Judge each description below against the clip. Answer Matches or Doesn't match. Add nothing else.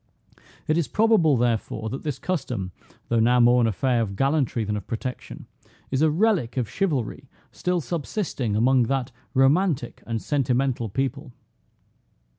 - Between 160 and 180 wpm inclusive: Doesn't match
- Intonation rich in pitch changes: Doesn't match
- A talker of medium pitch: Doesn't match